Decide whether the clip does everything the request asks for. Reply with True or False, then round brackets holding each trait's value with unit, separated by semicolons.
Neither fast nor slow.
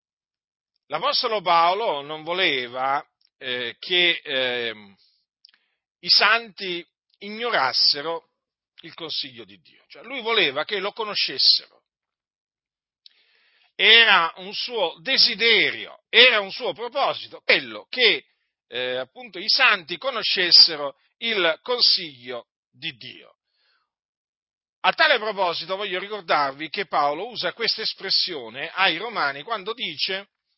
False (105 wpm)